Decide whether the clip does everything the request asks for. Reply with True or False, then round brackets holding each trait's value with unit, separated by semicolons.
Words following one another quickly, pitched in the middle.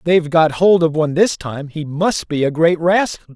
True (250 wpm; 165 Hz)